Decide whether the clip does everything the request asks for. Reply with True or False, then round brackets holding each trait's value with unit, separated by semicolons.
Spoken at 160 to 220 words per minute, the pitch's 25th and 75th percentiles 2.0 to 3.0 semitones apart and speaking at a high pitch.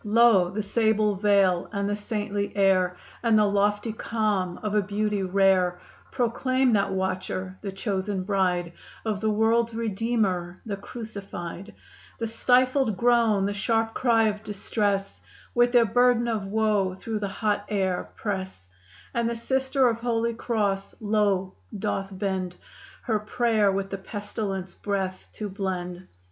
False (145 wpm; 2.7 semitones; 205 Hz)